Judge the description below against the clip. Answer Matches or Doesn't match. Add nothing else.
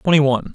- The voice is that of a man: Matches